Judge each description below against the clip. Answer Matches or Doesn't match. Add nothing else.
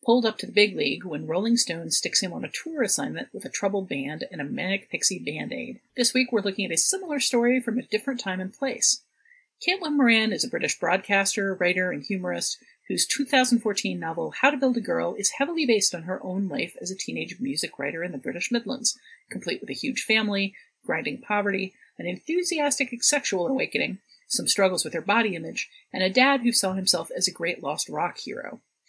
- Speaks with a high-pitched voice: Matches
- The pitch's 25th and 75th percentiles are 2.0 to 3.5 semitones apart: Doesn't match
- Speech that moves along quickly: Matches